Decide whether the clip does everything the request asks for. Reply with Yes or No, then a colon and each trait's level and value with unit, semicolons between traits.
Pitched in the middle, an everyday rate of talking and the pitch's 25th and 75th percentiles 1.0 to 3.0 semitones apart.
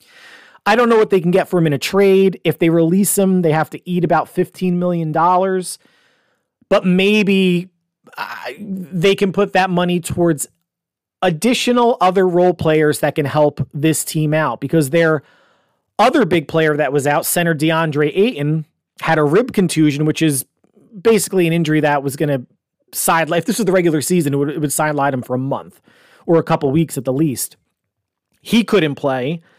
No: medium, 165 Hz; average, 190 wpm; average, 3.6 semitones